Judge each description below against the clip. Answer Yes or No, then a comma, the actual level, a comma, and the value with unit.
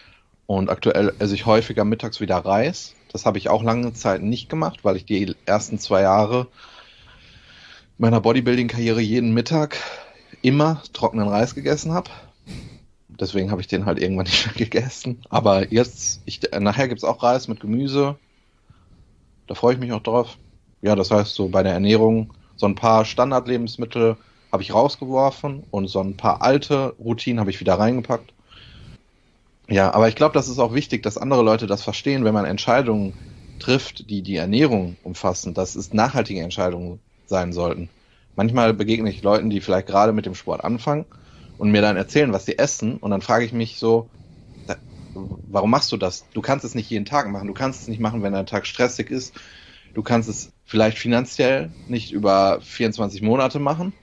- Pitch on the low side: Yes, low, 110 Hz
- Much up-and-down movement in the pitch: No, average, 3.5 semitones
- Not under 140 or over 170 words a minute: No, average, 180 wpm